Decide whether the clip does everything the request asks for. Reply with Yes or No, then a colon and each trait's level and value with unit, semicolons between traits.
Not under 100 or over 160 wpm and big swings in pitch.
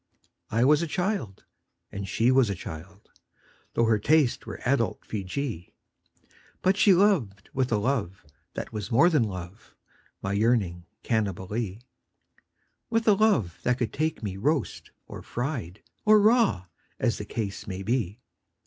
Yes: average, 155 wpm; wide, 6.8 semitones